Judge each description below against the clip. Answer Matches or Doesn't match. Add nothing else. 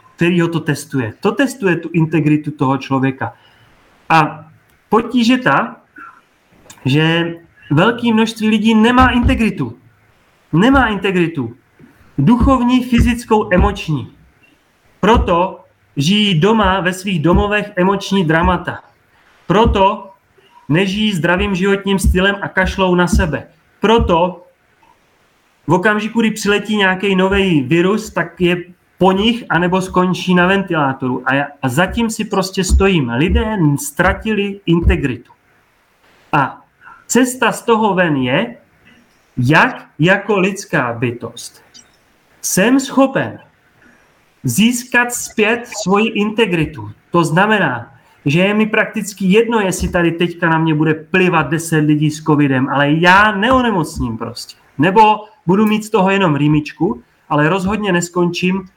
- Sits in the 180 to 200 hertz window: Matches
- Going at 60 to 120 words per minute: Matches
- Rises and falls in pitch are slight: Doesn't match